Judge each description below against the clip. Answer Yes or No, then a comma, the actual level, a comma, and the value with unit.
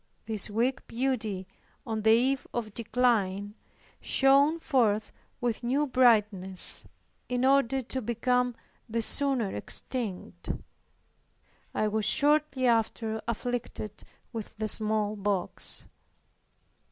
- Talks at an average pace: No, slow, 100 wpm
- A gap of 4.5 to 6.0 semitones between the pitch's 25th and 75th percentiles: No, average, 3.3 semitones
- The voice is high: Yes, high, 230 Hz